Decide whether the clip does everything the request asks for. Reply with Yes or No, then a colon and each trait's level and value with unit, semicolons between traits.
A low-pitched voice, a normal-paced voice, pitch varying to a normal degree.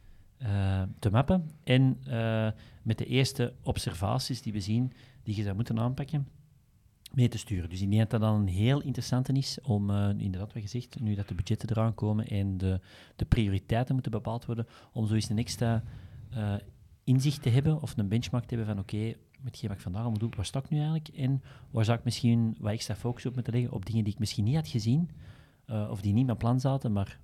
No: low, 115 Hz; fast, 225 wpm; average, 3.2 semitones